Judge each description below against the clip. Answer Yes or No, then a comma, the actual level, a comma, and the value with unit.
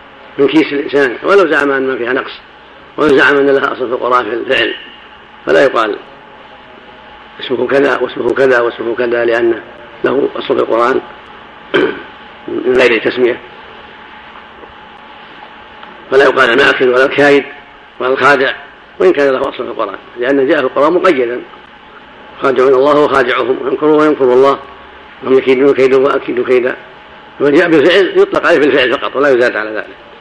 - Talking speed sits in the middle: No, fast, 145 wpm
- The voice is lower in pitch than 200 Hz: Yes, medium, 140 Hz